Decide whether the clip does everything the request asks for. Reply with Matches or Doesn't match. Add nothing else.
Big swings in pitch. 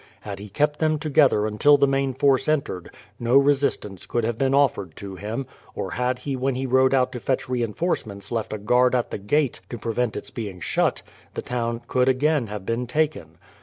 Doesn't match